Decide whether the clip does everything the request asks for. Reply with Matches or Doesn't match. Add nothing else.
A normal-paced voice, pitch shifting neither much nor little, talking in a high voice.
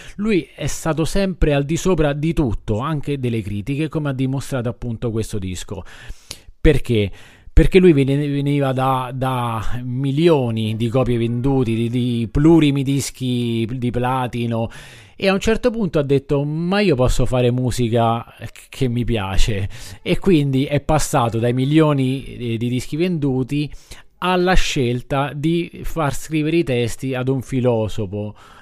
Doesn't match